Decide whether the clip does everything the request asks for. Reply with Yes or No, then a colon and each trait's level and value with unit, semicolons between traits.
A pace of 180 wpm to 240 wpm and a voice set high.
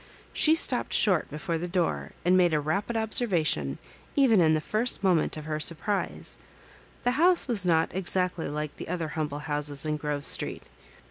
No: average, 185 wpm; medium, 165 Hz